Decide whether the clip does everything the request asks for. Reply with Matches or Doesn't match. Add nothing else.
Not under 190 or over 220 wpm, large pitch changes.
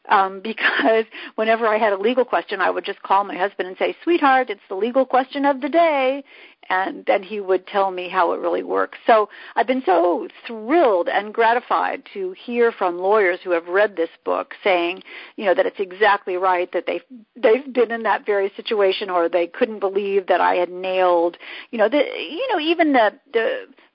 Matches